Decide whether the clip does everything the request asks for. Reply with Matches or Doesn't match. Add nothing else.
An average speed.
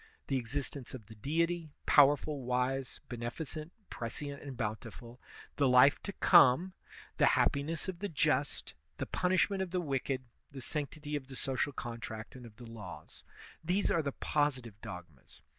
Matches